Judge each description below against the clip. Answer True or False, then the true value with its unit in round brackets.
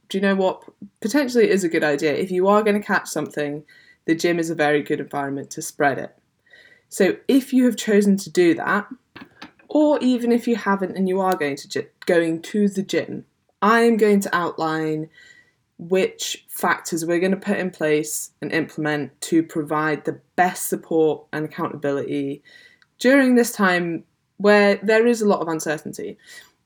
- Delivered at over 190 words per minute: False (180 wpm)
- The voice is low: False (185 Hz)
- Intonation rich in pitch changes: True (5.8 semitones)